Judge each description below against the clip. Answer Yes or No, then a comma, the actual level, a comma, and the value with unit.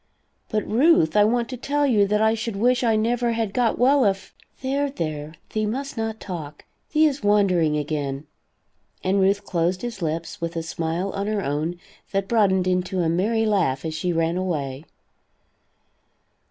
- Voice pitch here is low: No, high, 195 Hz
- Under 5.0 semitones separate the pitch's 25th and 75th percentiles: No, wide, 5.5 semitones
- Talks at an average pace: Yes, average, 180 wpm